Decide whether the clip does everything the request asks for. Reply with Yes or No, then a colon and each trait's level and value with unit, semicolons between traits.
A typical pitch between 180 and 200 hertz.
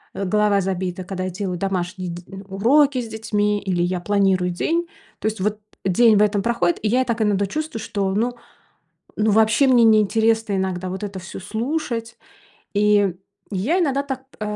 No: high, 210 Hz